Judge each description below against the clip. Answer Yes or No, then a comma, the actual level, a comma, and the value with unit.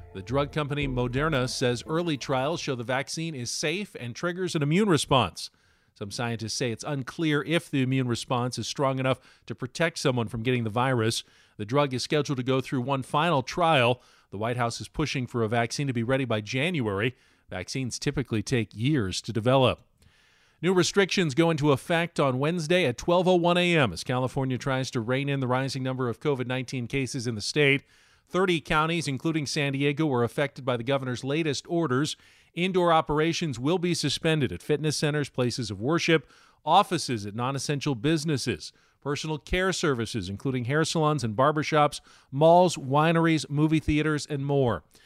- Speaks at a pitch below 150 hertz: Yes, medium, 140 Hz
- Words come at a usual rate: Yes, average, 175 wpm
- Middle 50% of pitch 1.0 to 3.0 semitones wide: No, average, 4.2 semitones